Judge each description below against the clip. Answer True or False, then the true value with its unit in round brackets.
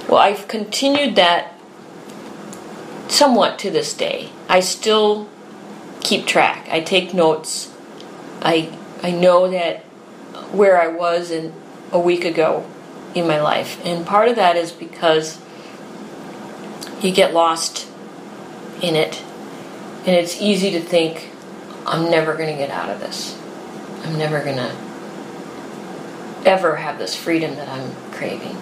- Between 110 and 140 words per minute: True (135 wpm)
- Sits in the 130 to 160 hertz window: False (170 Hz)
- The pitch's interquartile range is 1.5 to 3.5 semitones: True (2.6 semitones)